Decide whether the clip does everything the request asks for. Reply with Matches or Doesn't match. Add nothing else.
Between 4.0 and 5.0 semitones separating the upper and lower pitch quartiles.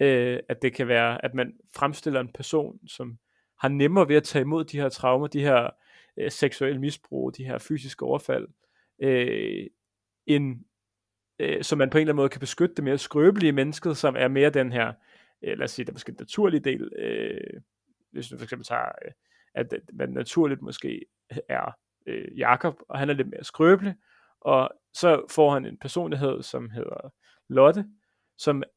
Doesn't match